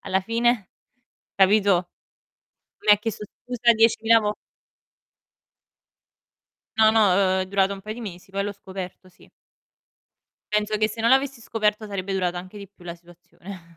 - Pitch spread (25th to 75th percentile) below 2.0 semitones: No, average, 2.8 semitones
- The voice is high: Yes, high, 200 Hz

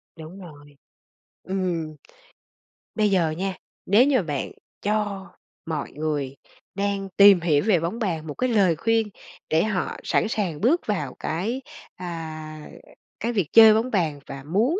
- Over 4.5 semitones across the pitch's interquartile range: Yes, average, 5.2 semitones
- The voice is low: No, medium, 185 Hz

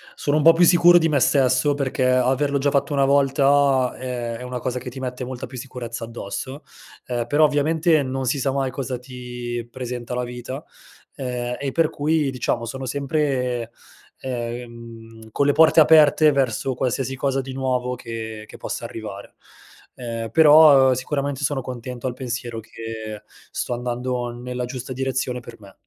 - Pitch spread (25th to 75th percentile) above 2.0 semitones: Yes, narrow, 2.4 semitones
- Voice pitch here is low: Yes, low, 130 Hz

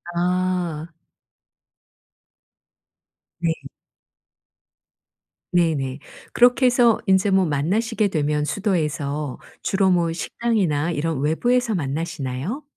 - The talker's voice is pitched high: No, medium, 175 Hz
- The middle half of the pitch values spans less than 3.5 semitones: No, average, 5.2 semitones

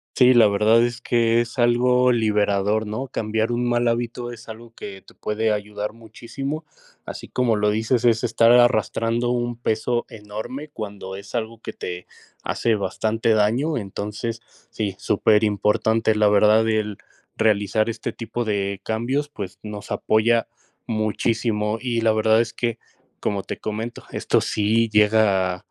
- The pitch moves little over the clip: Yes, narrow, 2.0 semitones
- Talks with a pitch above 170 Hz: No, low, 110 Hz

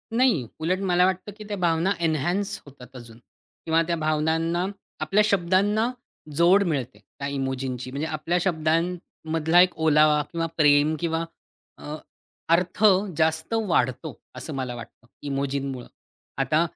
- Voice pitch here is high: No, medium, 160 Hz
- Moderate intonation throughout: Yes, average, 3.9 semitones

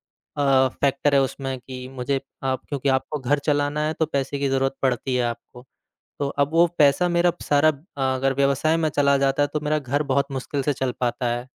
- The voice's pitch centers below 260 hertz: Yes, medium, 140 Hz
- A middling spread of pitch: No, narrow, 1.6 semitones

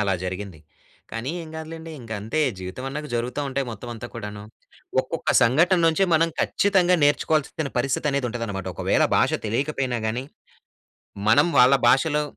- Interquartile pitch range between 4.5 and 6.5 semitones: Yes, wide, 5.4 semitones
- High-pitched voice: No, low, 130 Hz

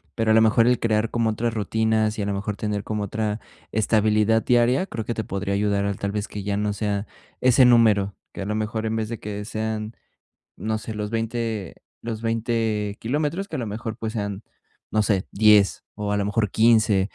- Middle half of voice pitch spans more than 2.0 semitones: No, narrow, 1.6 semitones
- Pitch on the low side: Yes, low, 110 Hz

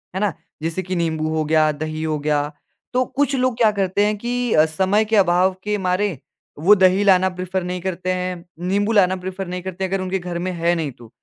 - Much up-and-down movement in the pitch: No, average, 3.3 semitones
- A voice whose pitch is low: No, medium, 185 Hz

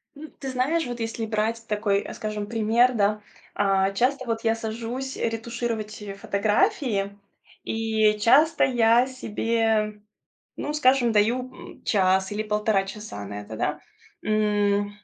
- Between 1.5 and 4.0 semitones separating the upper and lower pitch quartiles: Yes, narrow, 2.6 semitones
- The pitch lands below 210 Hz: No, high, 220 Hz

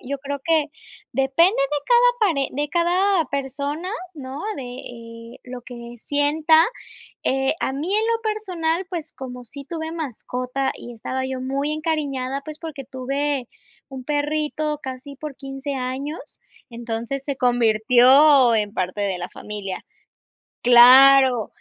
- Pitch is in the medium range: No, very high, 275 Hz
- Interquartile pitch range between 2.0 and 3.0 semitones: No, average, 3.5 semitones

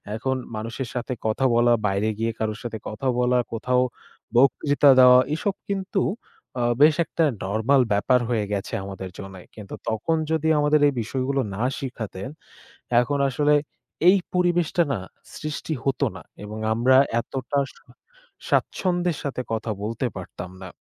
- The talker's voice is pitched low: Yes, low, 125 Hz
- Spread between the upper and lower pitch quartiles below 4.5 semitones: No, average, 5.1 semitones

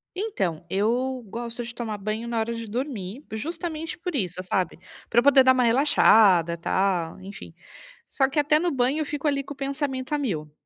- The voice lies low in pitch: No, high, 245 Hz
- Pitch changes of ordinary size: No, wide, 5.8 semitones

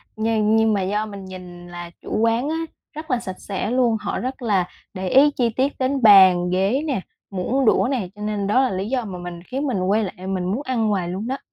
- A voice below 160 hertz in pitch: No, high, 210 Hz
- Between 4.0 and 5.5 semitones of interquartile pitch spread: Yes, average, 5.1 semitones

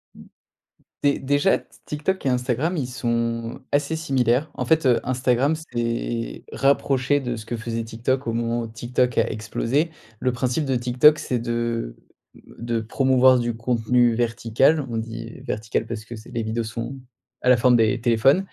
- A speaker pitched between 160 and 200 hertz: No, low, 120 Hz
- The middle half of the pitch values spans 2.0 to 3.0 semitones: Yes, narrow, 2.5 semitones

